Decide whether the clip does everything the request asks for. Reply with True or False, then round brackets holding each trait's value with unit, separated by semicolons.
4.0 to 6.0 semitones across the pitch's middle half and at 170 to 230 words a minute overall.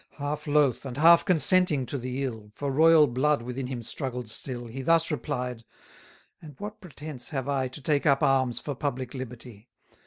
False (3.2 semitones; 180 wpm)